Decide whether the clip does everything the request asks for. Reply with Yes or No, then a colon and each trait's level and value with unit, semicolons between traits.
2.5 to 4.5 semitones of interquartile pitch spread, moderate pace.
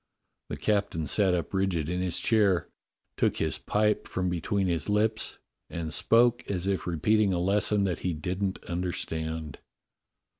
Yes: average, 3.3 semitones; average, 150 wpm